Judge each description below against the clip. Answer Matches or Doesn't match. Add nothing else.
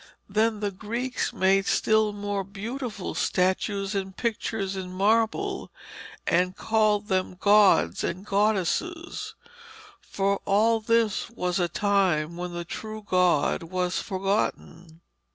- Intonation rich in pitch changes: Doesn't match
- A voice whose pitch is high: Matches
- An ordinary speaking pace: Doesn't match